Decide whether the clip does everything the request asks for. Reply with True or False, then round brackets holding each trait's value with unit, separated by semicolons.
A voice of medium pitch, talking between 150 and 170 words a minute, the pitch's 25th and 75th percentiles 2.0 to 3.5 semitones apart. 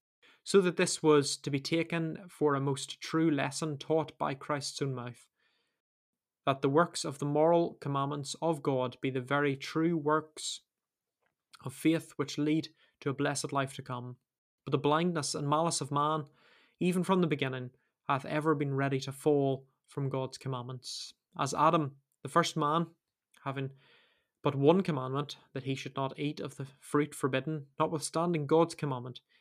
True (145 Hz; 165 wpm; 2.6 semitones)